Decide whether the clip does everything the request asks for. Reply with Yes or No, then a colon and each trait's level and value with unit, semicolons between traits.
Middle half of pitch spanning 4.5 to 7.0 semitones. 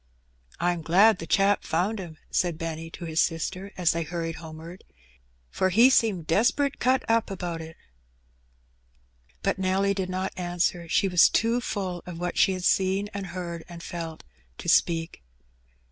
No: average, 2.9 semitones